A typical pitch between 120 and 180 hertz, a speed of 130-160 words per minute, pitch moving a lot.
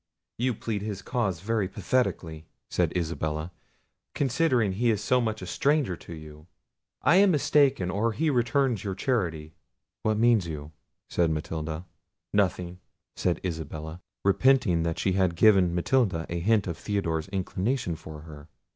No: very low, 95 Hz; average, 145 wpm; wide, 6.1 semitones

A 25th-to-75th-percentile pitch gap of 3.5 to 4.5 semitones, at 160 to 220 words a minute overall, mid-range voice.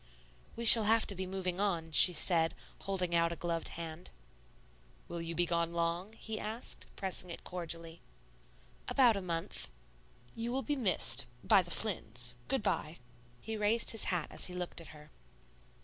Yes: average, 4.0 semitones; average, 170 wpm; medium, 180 Hz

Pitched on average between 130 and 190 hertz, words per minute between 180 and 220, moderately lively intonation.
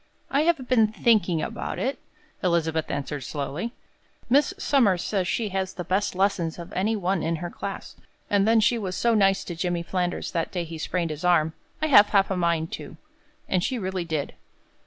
Yes: medium, 185 Hz; average, 195 wpm; average, 4.1 semitones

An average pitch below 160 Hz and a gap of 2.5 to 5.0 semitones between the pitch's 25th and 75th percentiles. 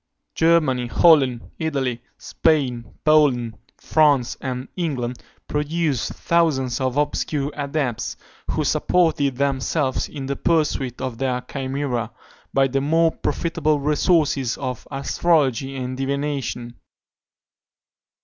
Yes: medium, 140 Hz; average, 3.1 semitones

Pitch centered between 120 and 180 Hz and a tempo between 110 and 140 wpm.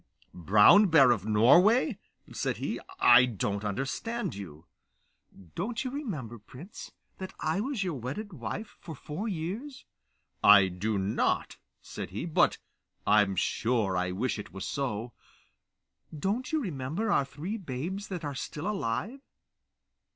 Yes: medium, 140 Hz; slow, 135 wpm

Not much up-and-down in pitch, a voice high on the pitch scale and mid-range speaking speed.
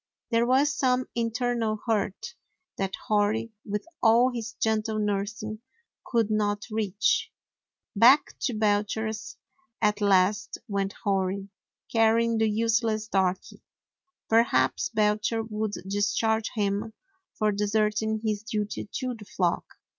No: narrow, 1.7 semitones; high, 215 Hz; slow, 115 wpm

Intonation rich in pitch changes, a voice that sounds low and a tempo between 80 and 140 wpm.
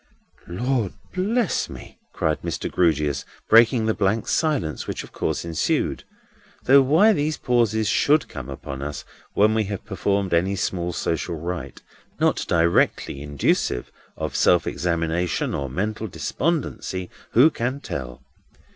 Yes: wide, 6.9 semitones; very low, 95 Hz; slow, 135 wpm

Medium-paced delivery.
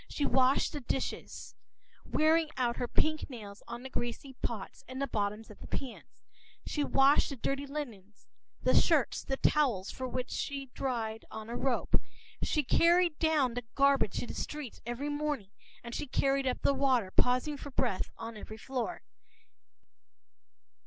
Yes: average, 165 wpm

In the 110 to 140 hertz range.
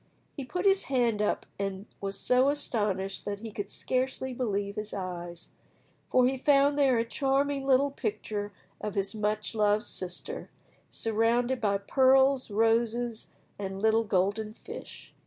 No: high, 225 Hz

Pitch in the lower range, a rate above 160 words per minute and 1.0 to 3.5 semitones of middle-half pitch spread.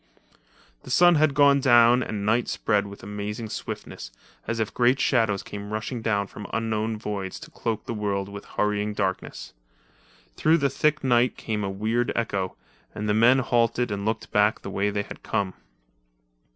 Yes: low, 110 Hz; average, 175 wpm; average, 2.9 semitones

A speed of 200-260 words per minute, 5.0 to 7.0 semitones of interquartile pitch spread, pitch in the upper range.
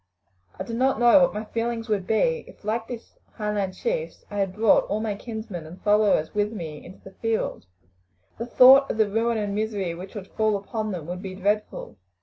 No: fast, 205 wpm; average, 2.7 semitones; high, 215 Hz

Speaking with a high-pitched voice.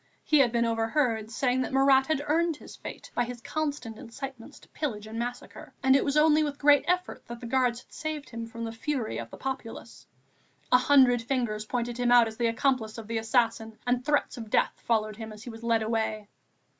Yes: high, 245 Hz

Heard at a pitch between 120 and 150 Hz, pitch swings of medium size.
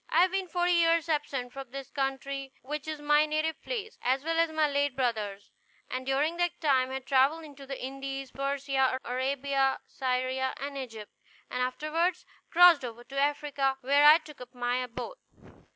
No: very high, 275 Hz; average, 3.0 semitones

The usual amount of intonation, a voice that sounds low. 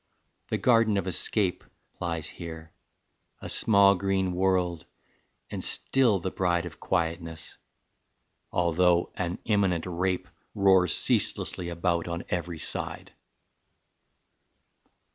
No: narrow, 2.0 semitones; very low, 90 Hz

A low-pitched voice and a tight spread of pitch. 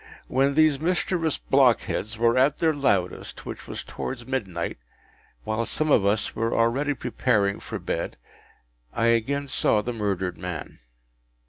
No: low, 120 Hz; average, 5.0 semitones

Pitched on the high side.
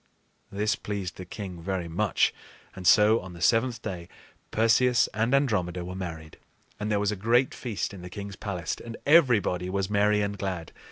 No: low, 100 Hz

